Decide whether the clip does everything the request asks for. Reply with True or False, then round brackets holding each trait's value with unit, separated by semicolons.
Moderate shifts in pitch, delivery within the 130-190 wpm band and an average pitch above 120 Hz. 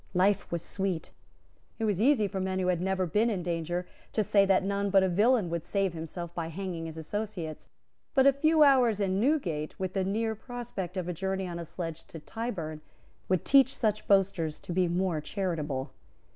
False (3.6 semitones; 200 wpm; 190 Hz)